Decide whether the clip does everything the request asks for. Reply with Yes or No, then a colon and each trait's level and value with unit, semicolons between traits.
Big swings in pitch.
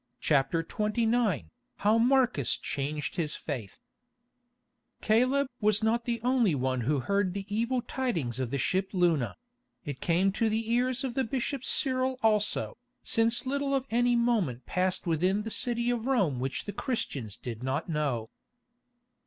Yes: wide, 8.4 semitones